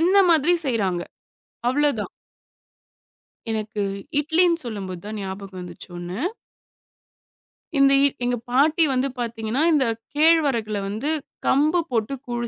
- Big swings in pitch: Yes, wide, 5.8 semitones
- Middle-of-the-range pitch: No, high, 245 Hz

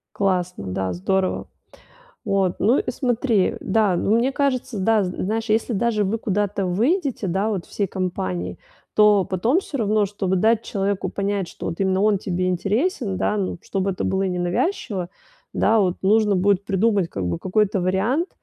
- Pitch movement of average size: Yes, average, 3.0 semitones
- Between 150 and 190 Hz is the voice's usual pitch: No, high, 200 Hz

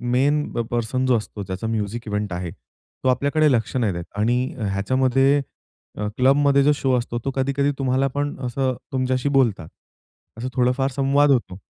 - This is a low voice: Yes, low, 130 Hz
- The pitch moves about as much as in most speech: Yes, average, 3.3 semitones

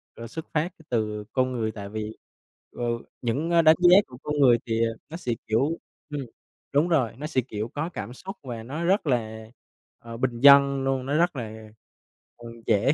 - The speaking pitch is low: Yes, low, 130 Hz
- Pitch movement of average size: Yes, average, 4.8 semitones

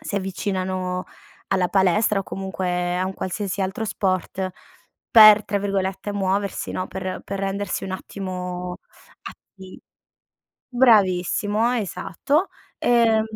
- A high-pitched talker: Yes, high, 195 Hz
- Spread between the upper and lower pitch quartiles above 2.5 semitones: No, narrow, 1.9 semitones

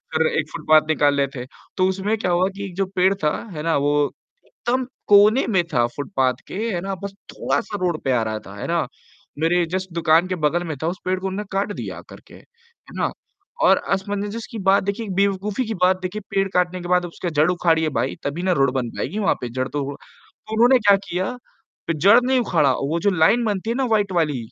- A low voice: No, medium, 185 Hz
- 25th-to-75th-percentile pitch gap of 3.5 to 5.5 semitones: Yes, average, 4.3 semitones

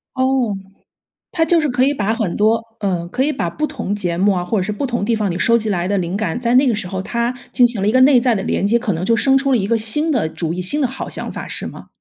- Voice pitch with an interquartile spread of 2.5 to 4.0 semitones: No, average, 4.8 semitones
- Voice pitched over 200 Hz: Yes, high, 225 Hz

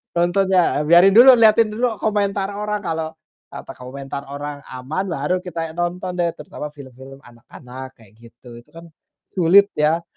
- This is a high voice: No, medium, 170 Hz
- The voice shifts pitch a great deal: Yes, wide, 6.1 semitones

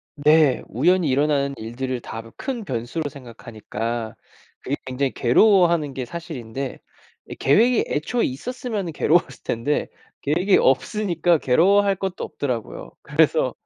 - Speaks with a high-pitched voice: No, medium, 145 Hz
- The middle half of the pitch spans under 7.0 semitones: Yes, wide, 5.9 semitones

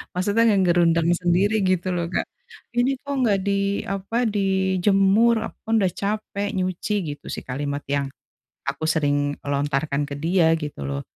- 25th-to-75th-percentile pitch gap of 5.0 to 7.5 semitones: Yes, wide, 5.5 semitones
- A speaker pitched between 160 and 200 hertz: Yes, medium, 185 Hz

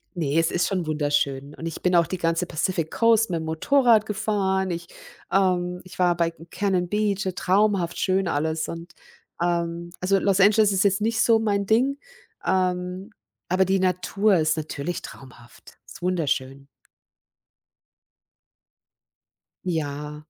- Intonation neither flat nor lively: Yes, average, 3.1 semitones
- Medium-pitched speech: Yes, medium, 180 Hz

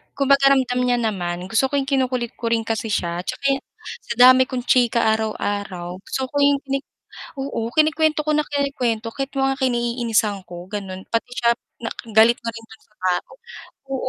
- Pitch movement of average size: Yes, average, 3.7 semitones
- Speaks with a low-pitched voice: No, high, 240 Hz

